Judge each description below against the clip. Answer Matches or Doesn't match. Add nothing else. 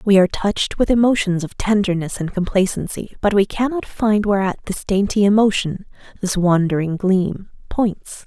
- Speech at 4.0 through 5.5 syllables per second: Matches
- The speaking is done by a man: Doesn't match